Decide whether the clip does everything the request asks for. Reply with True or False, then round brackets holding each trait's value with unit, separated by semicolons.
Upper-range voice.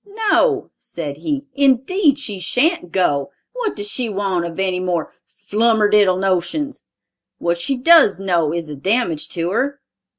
True (205 Hz)